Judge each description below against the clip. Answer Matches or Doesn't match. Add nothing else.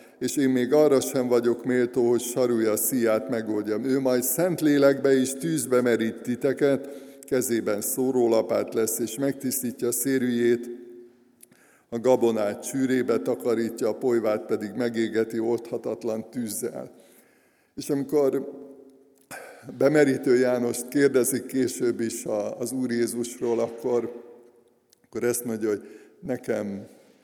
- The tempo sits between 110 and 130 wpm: Matches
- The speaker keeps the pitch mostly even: Matches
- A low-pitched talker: Matches